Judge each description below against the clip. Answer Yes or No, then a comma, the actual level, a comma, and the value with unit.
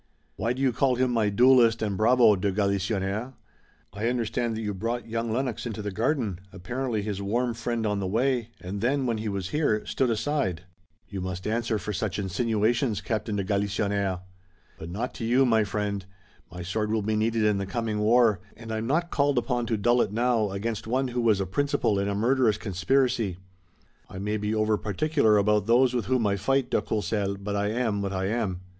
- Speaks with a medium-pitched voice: No, low, 110 Hz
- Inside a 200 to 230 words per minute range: Yes, fast, 205 wpm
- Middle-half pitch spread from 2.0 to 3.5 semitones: Yes, average, 3.1 semitones